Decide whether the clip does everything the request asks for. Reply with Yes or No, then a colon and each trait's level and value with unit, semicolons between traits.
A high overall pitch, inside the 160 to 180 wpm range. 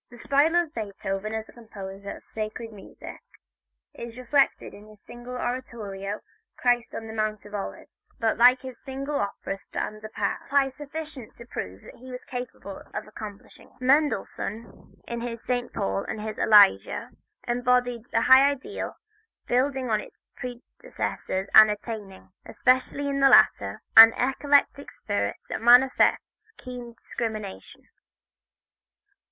No: high, 235 Hz; average, 140 wpm